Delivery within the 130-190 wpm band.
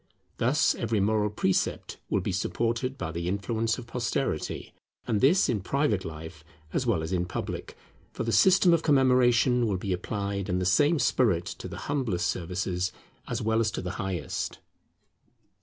Yes: average, 170 wpm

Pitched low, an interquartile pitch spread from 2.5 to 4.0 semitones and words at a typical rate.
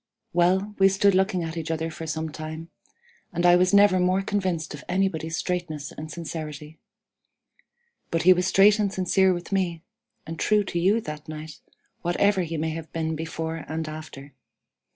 No: medium, 170 Hz; average, 3.0 semitones; average, 175 wpm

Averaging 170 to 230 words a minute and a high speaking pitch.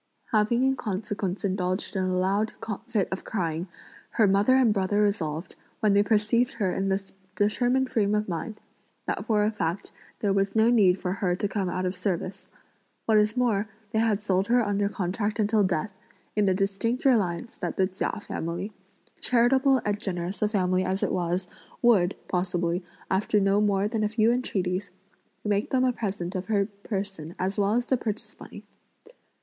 Yes: average, 180 wpm; high, 200 Hz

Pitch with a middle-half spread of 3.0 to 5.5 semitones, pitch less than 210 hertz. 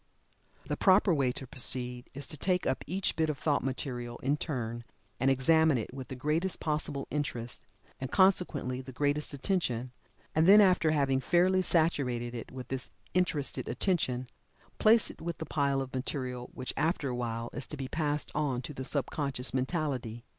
Yes: average, 3.9 semitones; medium, 140 Hz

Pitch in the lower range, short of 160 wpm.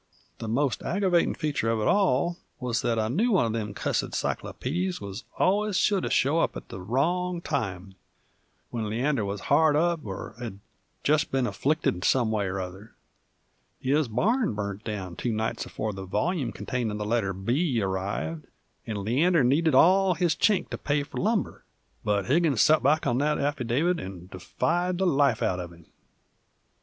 No: low, 125 Hz; average, 175 wpm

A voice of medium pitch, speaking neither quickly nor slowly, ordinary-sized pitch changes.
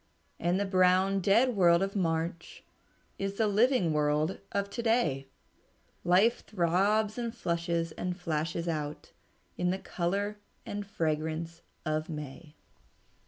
No: medium, 180 Hz; slow, 125 wpm; average, 3.6 semitones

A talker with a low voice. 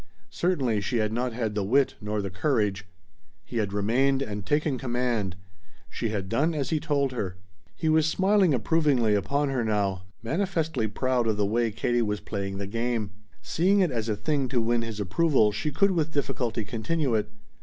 Yes: low, 120 Hz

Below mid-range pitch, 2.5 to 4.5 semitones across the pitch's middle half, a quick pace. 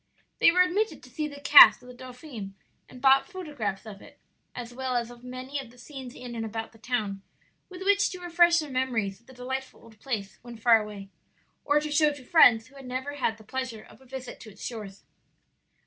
No: very high, 250 Hz; average, 4.2 semitones; fast, 225 wpm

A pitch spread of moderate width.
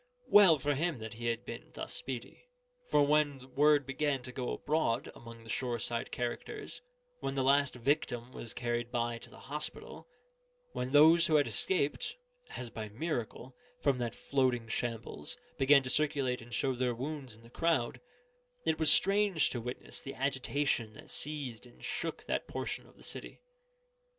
Yes: average, 3.7 semitones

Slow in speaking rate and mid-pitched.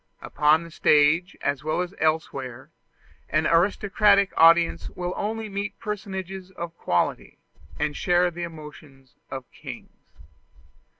Yes: slow, 120 wpm; medium, 170 Hz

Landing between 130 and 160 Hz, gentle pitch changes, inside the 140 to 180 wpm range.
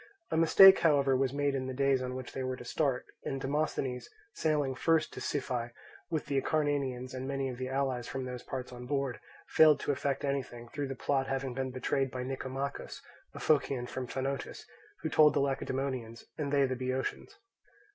No: low, 135 Hz; narrow, 1.6 semitones; average, 195 wpm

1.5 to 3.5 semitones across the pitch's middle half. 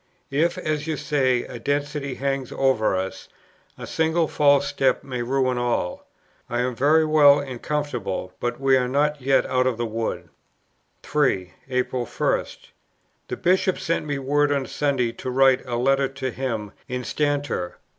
Yes: average, 2.8 semitones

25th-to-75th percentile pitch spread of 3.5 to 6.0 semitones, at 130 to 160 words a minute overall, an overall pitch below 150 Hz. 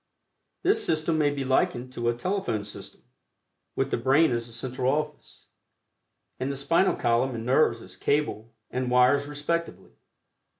Yes: average, 4.0 semitones; average, 155 wpm; low, 135 Hz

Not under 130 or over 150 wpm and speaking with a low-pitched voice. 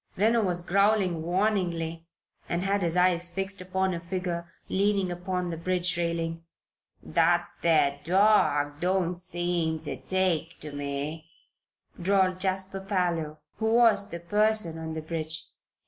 No: slow, 135 wpm; medium, 175 Hz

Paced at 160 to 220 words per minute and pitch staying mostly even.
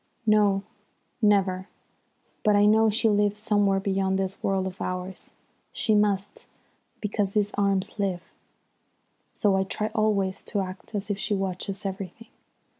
No: average, 140 wpm; narrow, 1.5 semitones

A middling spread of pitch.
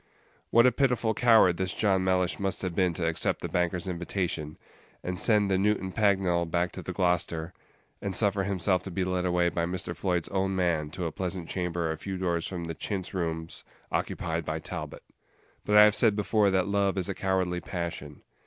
No: narrow, 2.2 semitones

